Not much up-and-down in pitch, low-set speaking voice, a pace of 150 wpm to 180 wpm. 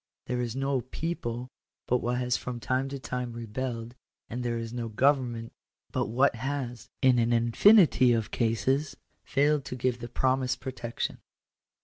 Yes: narrow, 2.0 semitones; low, 125 Hz; average, 160 wpm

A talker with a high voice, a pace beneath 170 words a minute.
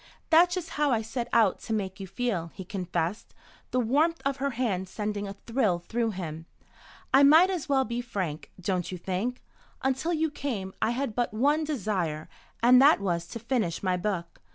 No: high, 225 Hz; average, 190 wpm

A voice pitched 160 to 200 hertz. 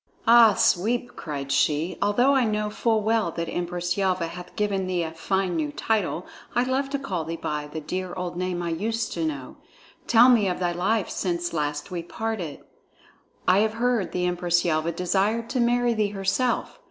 Yes: medium, 185 Hz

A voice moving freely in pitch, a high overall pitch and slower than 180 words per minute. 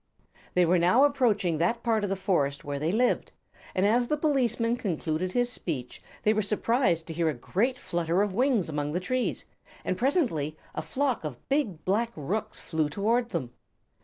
No: wide, 6.7 semitones; high, 195 Hz; average, 185 wpm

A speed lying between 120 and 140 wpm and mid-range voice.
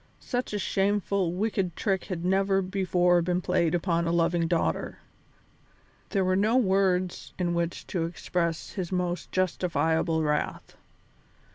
Yes: slow, 135 wpm; medium, 180 Hz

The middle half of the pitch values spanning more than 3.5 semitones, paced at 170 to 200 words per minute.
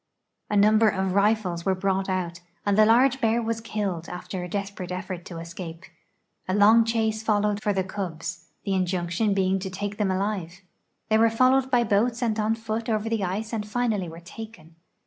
No: average, 3.1 semitones; average, 190 wpm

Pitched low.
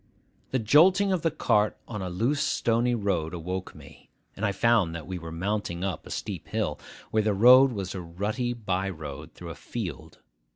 Yes: low, 100 Hz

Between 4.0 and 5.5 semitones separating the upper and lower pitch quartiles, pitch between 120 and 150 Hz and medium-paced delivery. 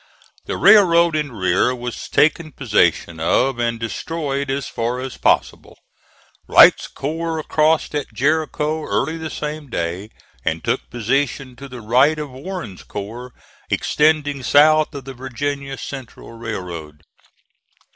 No: average, 4.6 semitones; low, 135 Hz; slow, 130 wpm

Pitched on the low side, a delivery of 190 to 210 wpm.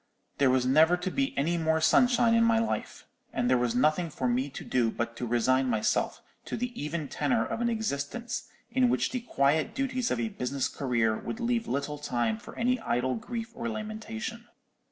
No: medium, 160 Hz; average, 195 wpm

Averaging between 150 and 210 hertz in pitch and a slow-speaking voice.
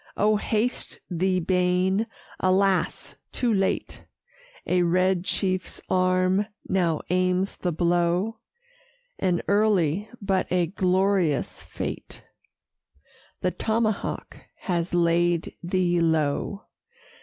Yes: medium, 185 Hz; slow, 95 wpm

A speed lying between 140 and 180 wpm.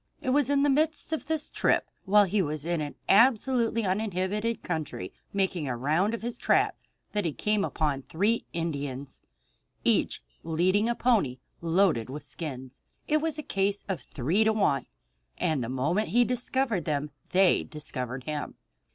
Yes: average, 165 wpm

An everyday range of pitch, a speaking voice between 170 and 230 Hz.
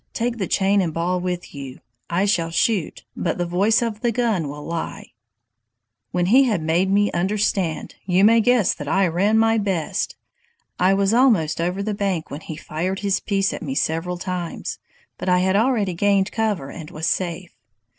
Yes: average, 3.5 semitones; high, 190 Hz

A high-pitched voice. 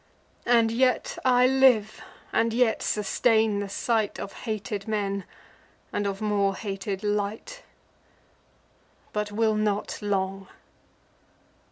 Yes: high, 210 Hz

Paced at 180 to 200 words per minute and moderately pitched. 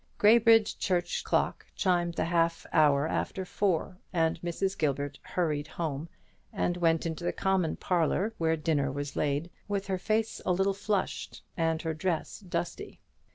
No: average, 155 wpm; medium, 170 Hz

